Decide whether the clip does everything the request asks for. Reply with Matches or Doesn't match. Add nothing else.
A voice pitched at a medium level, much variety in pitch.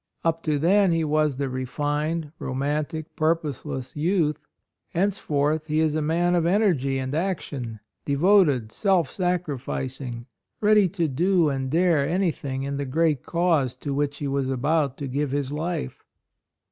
Doesn't match